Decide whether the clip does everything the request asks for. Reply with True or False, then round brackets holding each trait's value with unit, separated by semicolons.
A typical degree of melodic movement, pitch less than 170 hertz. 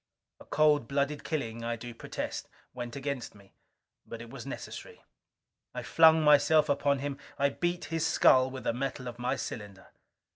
True (3.8 semitones; 135 Hz)